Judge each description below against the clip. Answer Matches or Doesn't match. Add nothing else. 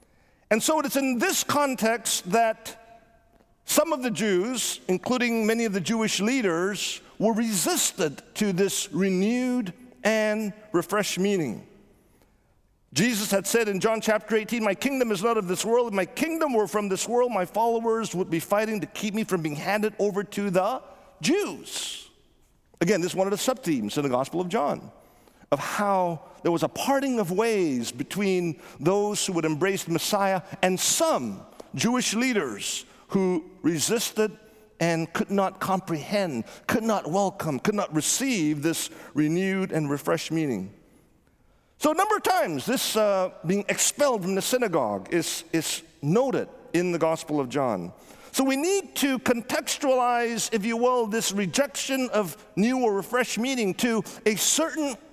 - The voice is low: Doesn't match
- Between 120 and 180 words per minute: Matches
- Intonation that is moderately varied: Matches